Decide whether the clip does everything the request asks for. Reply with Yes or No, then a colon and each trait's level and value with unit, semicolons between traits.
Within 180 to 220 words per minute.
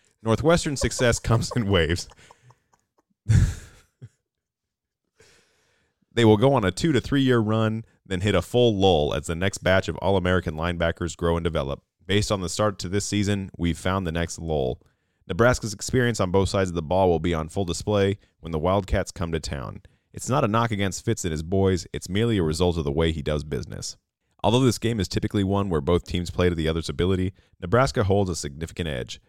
Yes: fast, 205 wpm